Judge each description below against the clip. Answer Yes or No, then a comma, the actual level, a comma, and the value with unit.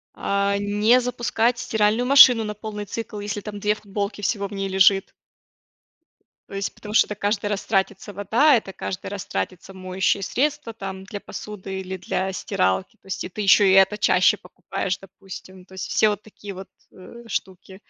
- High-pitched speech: Yes, high, 200 Hz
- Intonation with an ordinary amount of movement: No, narrow, 1.8 semitones